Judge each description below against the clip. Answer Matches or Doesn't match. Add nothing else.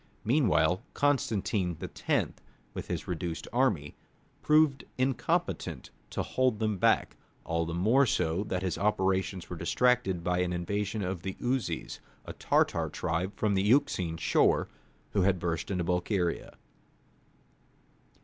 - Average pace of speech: Doesn't match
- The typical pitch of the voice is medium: Doesn't match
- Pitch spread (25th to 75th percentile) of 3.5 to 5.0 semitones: Matches